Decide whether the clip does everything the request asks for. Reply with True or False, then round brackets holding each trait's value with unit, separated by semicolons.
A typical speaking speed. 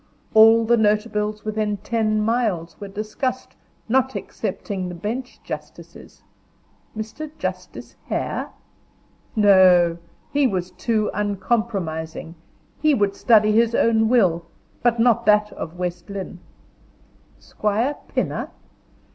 False (110 wpm)